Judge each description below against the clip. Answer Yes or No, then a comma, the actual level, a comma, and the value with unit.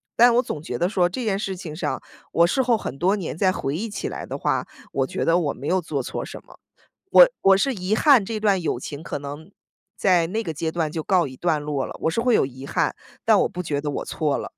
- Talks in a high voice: No, medium, 175 Hz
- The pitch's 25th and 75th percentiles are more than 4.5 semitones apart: Yes, average, 5.2 semitones